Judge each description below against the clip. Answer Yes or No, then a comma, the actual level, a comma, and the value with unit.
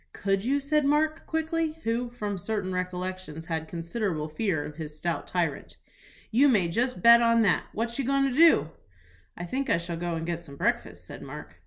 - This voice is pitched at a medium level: No, high, 195 Hz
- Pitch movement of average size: No, wide, 7.1 semitones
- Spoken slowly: No, average, 195 wpm